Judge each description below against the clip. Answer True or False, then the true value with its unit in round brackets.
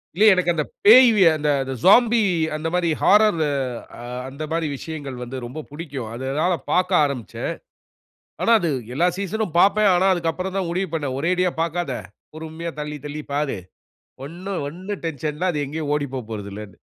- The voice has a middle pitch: True (165 Hz)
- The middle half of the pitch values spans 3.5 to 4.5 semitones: True (4.2 semitones)